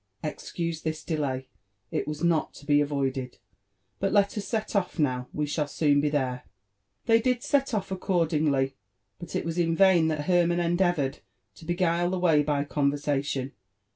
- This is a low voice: No, medium, 155 Hz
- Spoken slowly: No, average, 170 wpm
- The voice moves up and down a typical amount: Yes, average, 3.6 semitones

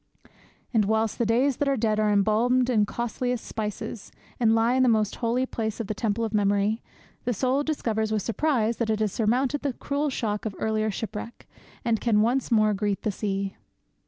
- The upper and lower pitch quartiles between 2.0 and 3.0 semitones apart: Yes, narrow, 2.6 semitones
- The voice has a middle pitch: No, high, 225 Hz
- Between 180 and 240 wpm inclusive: Yes, average, 195 wpm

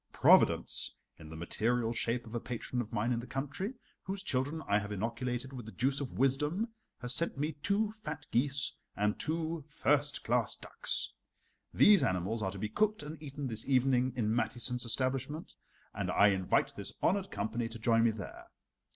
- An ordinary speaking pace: Yes, average, 180 wpm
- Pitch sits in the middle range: No, low, 125 Hz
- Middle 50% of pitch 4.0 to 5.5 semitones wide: Yes, average, 4.7 semitones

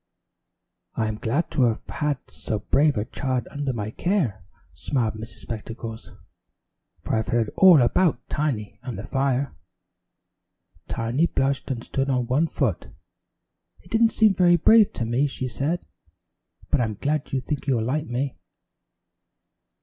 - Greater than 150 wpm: No, average, 140 wpm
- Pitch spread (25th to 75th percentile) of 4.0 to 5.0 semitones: Yes, average, 4.6 semitones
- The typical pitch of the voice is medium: No, low, 130 Hz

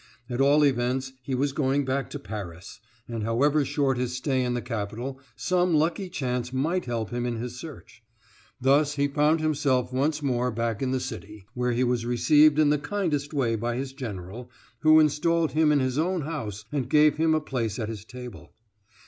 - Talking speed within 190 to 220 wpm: Yes, average, 195 wpm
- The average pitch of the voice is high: No, low, 130 Hz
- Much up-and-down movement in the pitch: No, average, 3.7 semitones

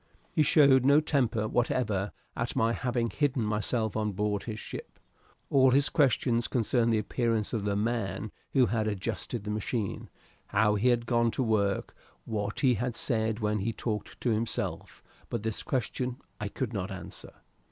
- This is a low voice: Yes, low, 115 Hz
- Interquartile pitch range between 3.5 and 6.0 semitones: No, average, 2.8 semitones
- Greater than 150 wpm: Yes, average, 170 wpm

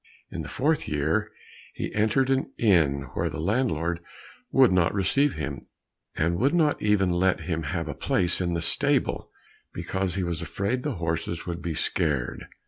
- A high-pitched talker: No, very low, 90 Hz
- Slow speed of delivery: No, average, 170 wpm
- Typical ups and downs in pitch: Yes, average, 4.9 semitones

